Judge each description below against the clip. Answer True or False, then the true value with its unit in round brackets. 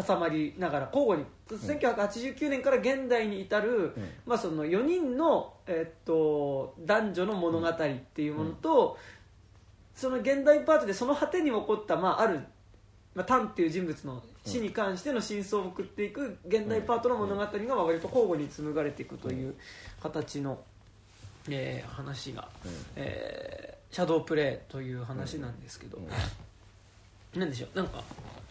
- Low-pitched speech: False (170 Hz)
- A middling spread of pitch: False (8.9 semitones)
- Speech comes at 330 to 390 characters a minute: False (285 characters per minute)